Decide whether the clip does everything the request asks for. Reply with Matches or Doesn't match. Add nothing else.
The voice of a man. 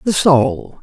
Matches